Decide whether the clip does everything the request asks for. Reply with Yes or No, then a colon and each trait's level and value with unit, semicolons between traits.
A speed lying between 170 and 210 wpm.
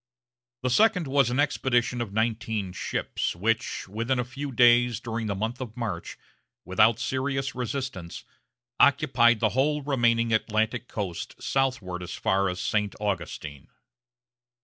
No: slow, 135 wpm